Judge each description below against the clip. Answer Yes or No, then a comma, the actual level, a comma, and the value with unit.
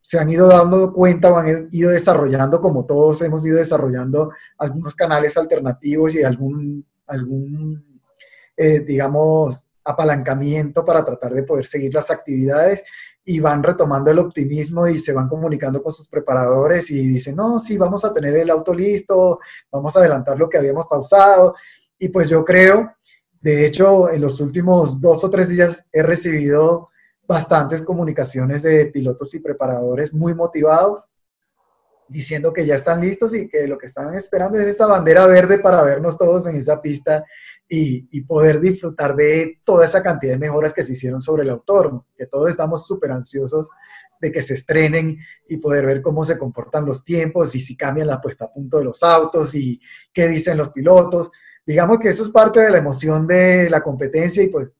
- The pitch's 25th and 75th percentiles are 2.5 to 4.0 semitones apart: Yes, average, 3.4 semitones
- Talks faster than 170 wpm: Yes, average, 180 wpm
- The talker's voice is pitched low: No, medium, 155 Hz